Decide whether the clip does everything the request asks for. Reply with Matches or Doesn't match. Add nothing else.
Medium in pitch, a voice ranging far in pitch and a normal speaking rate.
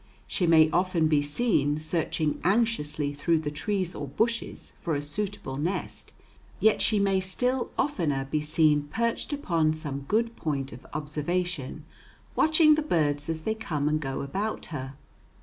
Matches